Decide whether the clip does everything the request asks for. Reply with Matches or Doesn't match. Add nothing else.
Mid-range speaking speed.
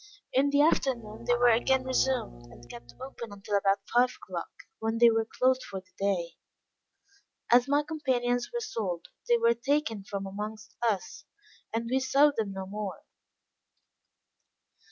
Matches